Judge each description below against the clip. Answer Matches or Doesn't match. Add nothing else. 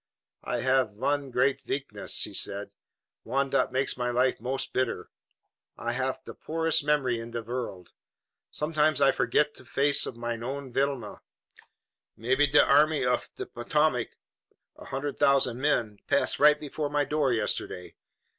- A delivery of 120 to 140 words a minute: Doesn't match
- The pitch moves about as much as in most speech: Matches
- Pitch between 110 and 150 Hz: Matches